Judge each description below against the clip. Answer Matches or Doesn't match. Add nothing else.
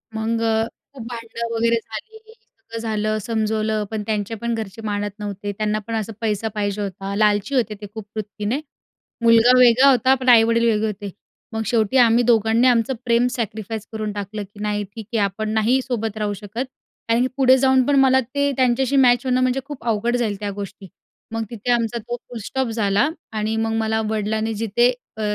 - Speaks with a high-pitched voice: Matches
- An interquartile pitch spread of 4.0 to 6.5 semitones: Doesn't match